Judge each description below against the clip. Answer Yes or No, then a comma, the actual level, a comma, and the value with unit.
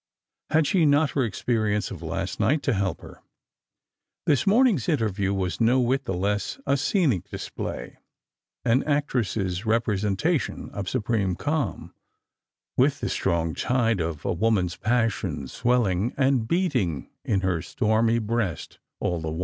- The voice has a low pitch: Yes, low, 115 Hz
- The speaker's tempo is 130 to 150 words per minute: Yes, average, 145 wpm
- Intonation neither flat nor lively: No, wide, 5.8 semitones